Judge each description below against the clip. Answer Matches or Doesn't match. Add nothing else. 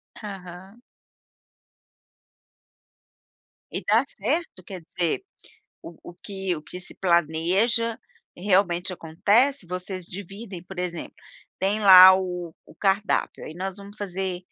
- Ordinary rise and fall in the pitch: Doesn't match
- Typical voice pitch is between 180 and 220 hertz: Matches